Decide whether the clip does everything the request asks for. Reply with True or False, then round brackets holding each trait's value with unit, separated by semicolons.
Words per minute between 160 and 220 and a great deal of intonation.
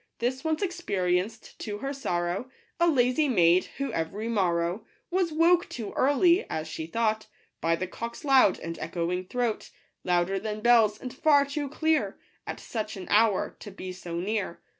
True (165 wpm; 7.0 semitones)